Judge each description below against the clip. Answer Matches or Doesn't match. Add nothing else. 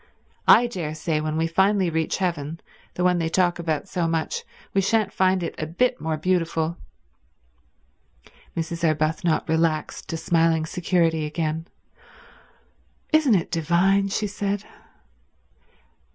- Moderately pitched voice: Matches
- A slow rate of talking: Matches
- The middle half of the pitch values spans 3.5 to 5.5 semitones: Doesn't match